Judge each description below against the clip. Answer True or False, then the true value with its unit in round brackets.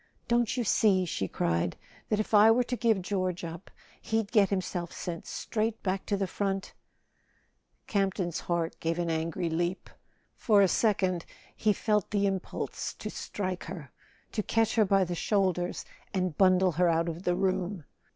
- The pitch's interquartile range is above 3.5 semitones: False (3.1 semitones)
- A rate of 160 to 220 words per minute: True (170 wpm)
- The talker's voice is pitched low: False (190 Hz)